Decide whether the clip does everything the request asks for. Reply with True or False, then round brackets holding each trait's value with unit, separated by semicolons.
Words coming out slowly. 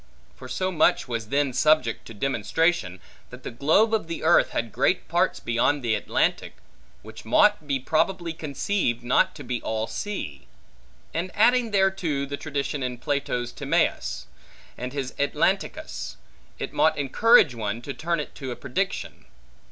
False (155 wpm)